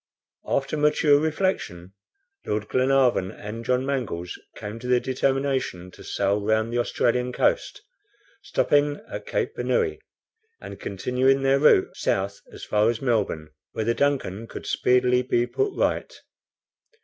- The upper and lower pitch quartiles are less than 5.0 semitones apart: Yes, average, 4.5 semitones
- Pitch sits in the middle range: No, low, 125 Hz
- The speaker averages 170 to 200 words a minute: No, slow, 135 wpm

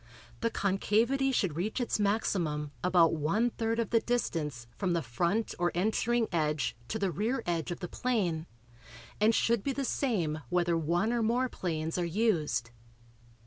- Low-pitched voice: No, high, 190 Hz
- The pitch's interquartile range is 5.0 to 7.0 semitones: Yes, wide, 5.6 semitones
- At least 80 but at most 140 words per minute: No, average, 165 wpm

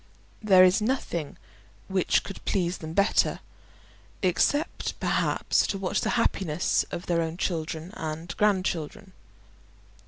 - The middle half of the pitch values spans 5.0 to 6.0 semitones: No, average, 3.3 semitones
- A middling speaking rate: No, slow, 120 wpm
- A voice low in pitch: No, medium, 180 Hz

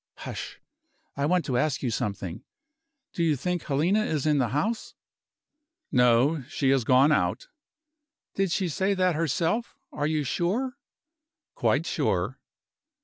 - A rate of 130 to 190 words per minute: Yes, average, 140 wpm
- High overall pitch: No, medium, 155 Hz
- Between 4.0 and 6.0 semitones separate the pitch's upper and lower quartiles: Yes, average, 5.2 semitones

